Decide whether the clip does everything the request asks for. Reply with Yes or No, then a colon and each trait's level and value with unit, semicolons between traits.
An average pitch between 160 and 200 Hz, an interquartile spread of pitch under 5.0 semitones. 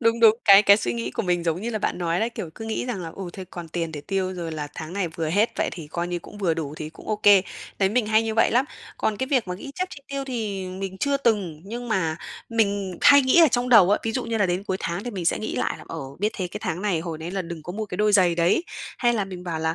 Yes: high, 195 Hz; average, 4.6 semitones